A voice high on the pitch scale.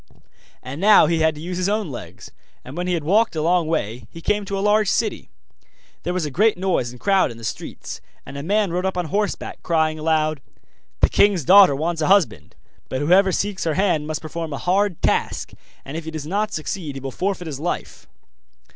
No: medium, 170 Hz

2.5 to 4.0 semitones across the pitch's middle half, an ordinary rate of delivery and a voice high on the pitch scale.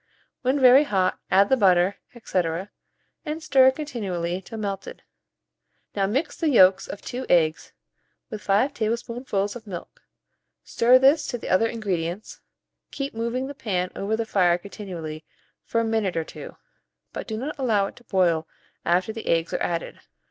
No: average, 5.1 semitones; average, 165 wpm; high, 210 Hz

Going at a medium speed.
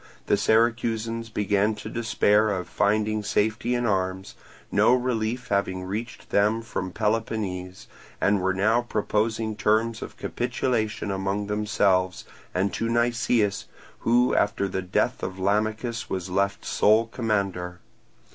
No: slow, 130 wpm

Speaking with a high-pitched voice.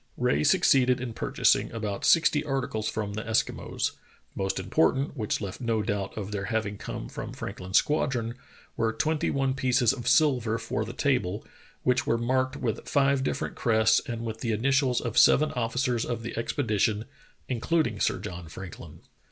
No: low, 115 Hz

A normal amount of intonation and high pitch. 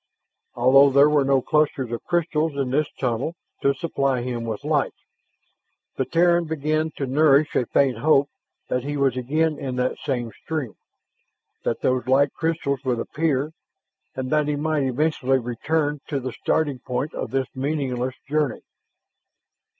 No: average, 3.0 semitones; medium, 140 Hz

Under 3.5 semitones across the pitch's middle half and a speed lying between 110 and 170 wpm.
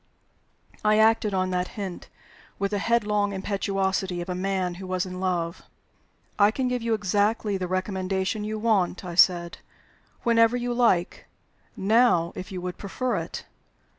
Yes: average, 2.8 semitones; average, 155 wpm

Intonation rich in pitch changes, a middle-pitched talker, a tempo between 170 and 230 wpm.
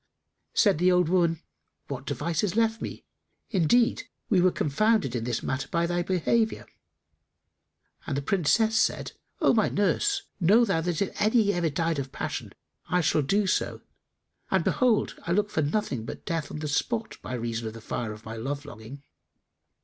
Yes: wide, 6.7 semitones; medium, 170 Hz; average, 180 wpm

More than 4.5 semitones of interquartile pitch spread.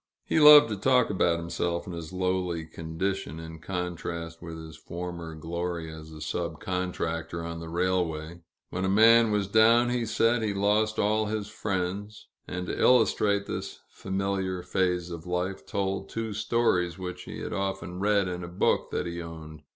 No: average, 3.4 semitones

